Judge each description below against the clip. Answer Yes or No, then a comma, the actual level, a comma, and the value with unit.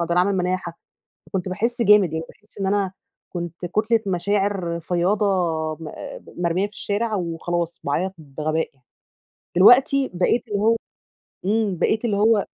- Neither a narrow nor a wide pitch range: Yes, average, 3.4 semitones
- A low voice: No, high, 190 Hz